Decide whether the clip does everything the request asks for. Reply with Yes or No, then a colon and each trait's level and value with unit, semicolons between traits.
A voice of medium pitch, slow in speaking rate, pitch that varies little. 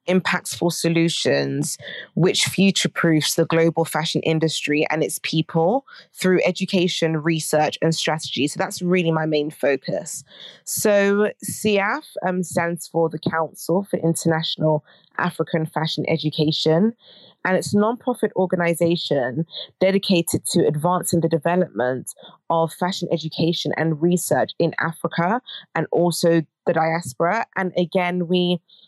Yes: medium, 165 Hz; slow, 125 wpm; narrow, 2.2 semitones